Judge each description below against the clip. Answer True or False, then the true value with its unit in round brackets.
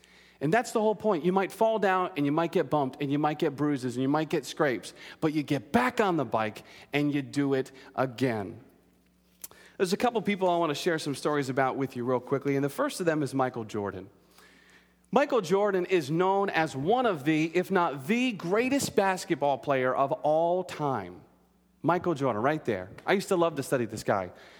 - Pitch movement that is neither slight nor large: False (5.7 semitones)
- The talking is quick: True (215 wpm)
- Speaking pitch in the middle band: True (150 Hz)